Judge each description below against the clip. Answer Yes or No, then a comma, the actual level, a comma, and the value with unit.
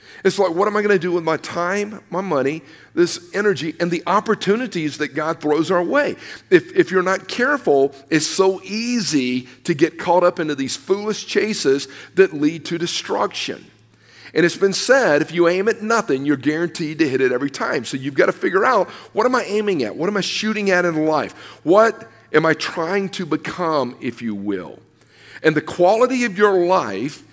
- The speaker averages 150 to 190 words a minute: No, average, 200 wpm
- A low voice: No, medium, 175 Hz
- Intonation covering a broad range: No, average, 4.9 semitones